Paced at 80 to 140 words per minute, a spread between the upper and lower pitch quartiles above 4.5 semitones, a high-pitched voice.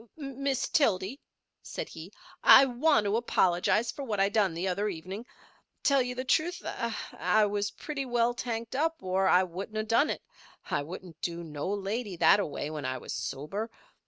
No: average, 185 wpm; average, 5.3 semitones; high, 210 Hz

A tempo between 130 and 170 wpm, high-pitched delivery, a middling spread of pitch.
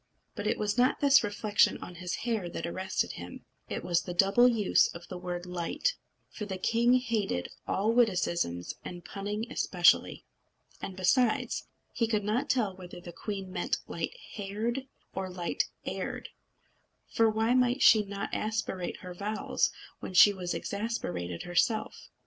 Yes: average, 155 wpm; high, 200 Hz; average, 4.0 semitones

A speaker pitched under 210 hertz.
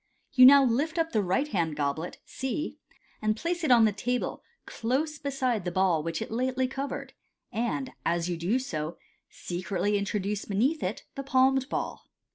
No: high, 230 Hz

